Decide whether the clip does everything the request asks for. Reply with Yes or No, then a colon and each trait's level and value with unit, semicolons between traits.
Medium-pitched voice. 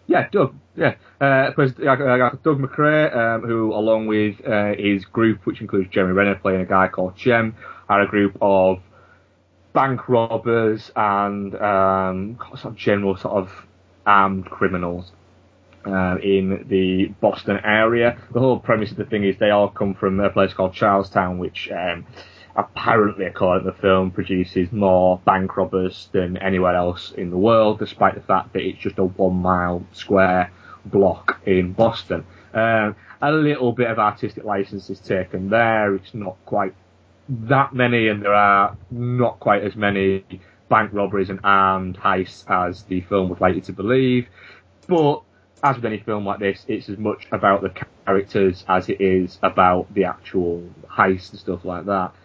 No: low, 100 Hz